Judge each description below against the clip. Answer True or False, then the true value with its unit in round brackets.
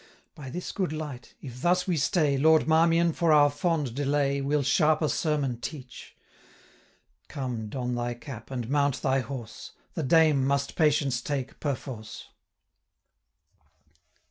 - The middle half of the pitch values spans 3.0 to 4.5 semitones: True (3.3 semitones)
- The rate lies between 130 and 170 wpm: True (140 wpm)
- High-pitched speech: False (140 Hz)